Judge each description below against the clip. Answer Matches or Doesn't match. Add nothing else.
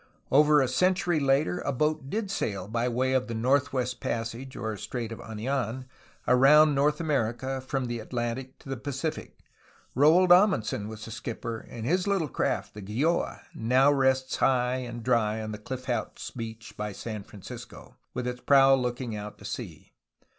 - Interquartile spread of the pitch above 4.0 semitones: Doesn't match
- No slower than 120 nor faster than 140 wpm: Doesn't match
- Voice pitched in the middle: Doesn't match